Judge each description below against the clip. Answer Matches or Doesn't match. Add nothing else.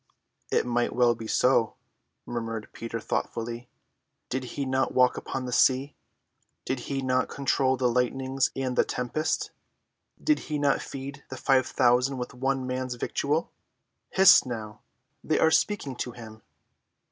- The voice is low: Matches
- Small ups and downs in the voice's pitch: Matches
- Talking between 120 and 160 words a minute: Matches